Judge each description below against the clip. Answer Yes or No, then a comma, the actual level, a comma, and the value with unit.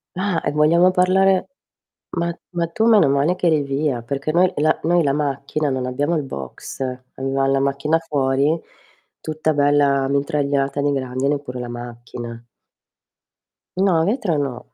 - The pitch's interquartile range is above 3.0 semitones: Yes, average, 3.5 semitones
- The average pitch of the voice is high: No, medium, 145 Hz